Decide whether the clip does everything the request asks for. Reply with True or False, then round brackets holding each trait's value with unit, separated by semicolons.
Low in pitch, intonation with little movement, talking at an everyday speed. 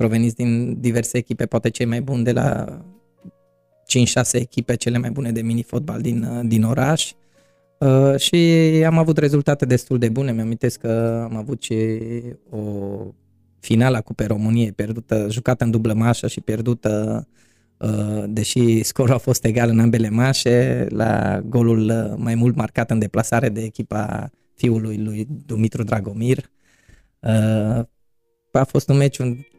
True (115 Hz; 2.1 semitones; 150 wpm)